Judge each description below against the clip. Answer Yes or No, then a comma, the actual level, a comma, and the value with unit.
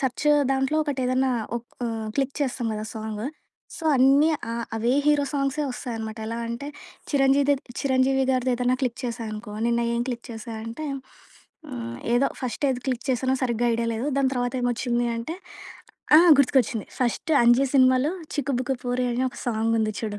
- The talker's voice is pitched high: Yes, very high, 250 Hz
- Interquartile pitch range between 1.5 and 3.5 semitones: Yes, narrow, 2.5 semitones